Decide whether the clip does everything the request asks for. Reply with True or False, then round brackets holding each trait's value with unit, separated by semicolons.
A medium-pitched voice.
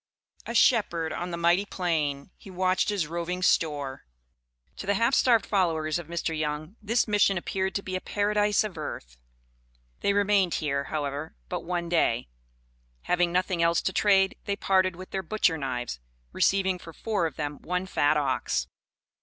True (175 Hz)